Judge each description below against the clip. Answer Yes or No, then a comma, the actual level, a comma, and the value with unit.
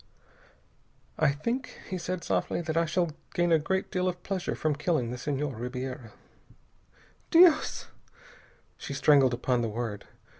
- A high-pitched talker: No, medium, 155 Hz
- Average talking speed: Yes, average, 150 wpm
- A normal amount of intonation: No, wide, 5.8 semitones